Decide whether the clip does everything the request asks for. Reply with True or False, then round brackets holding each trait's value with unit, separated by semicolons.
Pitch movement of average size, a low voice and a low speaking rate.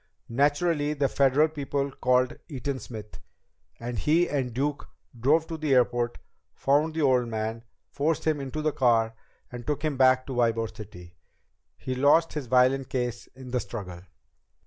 False (3.5 semitones; 130 Hz; 160 wpm)